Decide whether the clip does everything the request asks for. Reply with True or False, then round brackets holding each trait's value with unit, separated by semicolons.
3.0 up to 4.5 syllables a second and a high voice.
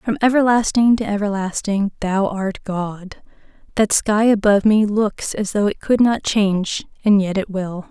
True (4.4 syllables/s; 205 Hz)